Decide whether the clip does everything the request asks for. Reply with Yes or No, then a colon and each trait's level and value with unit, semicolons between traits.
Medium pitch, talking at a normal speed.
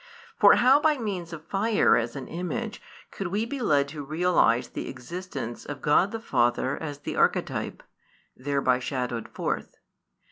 Yes: medium, 160 Hz; average, 155 wpm